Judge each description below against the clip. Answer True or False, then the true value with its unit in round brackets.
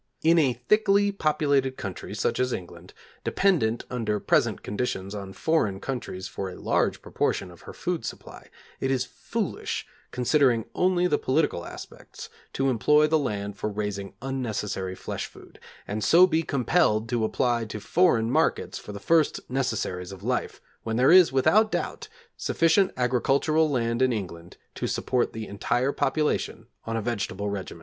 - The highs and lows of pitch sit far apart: True (6.4 semitones)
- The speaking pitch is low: True (125 Hz)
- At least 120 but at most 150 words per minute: False (160 wpm)